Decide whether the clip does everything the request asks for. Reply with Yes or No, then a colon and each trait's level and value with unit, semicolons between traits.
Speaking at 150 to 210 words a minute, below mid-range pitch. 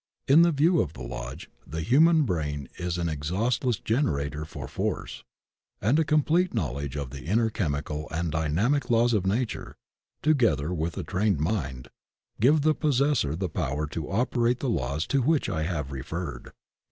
Yes: average, 165 wpm; very low, 90 Hz